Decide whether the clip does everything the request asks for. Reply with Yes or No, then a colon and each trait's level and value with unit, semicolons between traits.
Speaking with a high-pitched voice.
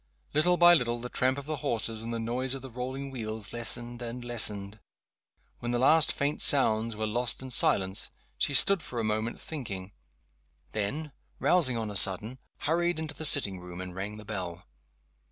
No: low, 120 Hz